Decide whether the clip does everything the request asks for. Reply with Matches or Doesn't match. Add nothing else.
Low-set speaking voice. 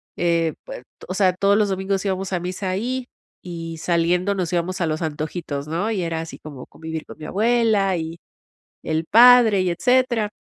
Doesn't match